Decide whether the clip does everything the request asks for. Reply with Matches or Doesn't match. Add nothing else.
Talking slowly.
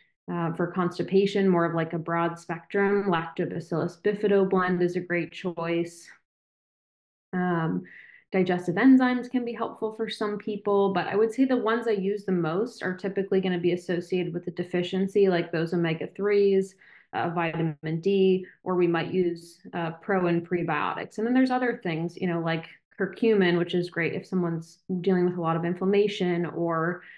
Doesn't match